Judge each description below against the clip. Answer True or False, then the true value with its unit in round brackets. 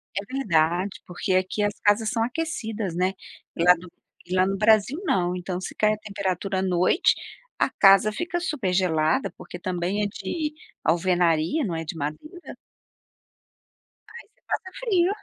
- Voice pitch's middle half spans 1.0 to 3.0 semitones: False (3.9 semitones)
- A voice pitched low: False (195 Hz)